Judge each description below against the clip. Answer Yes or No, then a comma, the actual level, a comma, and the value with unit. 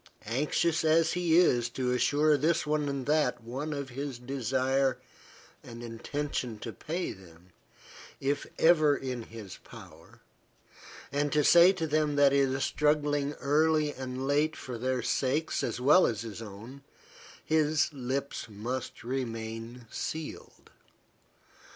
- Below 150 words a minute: Yes, slow, 135 wpm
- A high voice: No, medium, 140 Hz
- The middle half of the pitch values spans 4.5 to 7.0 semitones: No, average, 3.7 semitones